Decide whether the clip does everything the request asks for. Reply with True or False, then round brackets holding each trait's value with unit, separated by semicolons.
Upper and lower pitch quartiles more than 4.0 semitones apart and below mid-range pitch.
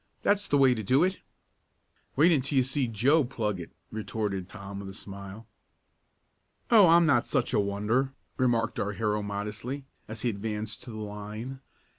True (4.5 semitones; 110 Hz)